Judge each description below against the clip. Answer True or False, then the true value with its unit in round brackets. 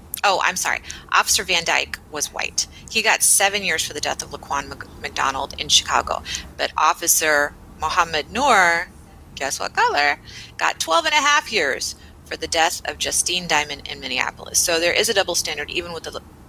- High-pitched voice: False (165 Hz)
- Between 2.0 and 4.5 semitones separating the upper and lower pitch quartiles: True (3.7 semitones)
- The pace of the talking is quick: False (180 wpm)